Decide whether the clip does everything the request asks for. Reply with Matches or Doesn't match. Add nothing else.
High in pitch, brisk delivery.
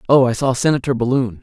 Doesn't match